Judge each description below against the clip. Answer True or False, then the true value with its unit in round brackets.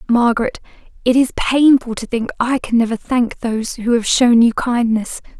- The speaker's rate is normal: True (180 wpm)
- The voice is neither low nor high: False (240 Hz)